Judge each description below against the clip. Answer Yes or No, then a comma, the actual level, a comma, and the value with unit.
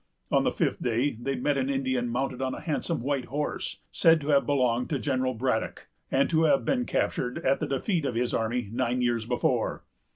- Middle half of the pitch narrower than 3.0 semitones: Yes, narrow, 2.6 semitones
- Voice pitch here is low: Yes, low, 130 Hz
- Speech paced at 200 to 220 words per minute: Yes, fast, 205 wpm